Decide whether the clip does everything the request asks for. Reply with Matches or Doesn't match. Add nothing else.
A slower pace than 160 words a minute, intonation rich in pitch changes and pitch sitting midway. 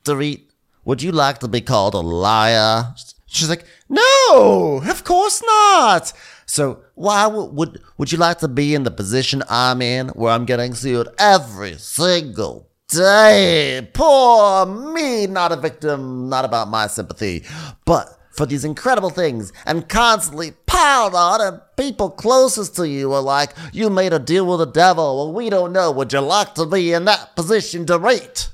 Doesn't match